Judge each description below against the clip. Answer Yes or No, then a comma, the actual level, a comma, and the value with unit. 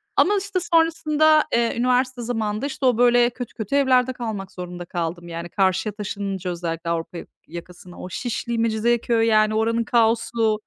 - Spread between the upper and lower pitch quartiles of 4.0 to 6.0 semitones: Yes, average, 4.8 semitones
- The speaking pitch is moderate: No, high, 225 Hz